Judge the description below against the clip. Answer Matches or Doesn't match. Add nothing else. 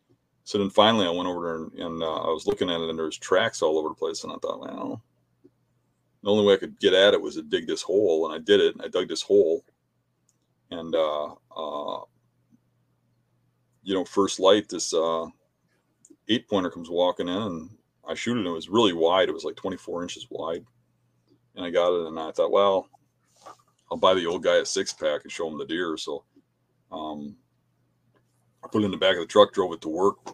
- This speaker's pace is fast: Matches